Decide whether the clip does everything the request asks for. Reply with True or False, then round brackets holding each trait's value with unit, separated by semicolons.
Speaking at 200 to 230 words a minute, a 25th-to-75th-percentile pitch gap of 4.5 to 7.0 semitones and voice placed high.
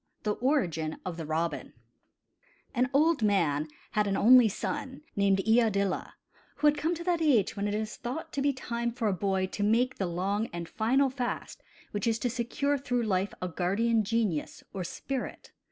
False (185 wpm; 5.1 semitones; 220 Hz)